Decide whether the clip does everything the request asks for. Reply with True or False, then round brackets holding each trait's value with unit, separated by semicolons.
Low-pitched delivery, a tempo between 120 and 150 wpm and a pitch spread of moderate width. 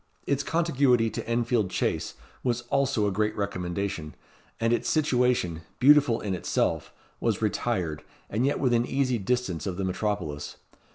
True (115 Hz; 145 wpm; 5.0 semitones)